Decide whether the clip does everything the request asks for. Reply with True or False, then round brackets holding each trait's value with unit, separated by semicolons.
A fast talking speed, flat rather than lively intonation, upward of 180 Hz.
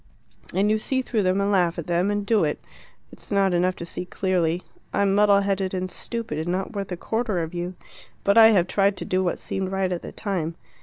True (235 wpm; 2.2 semitones; 190 Hz)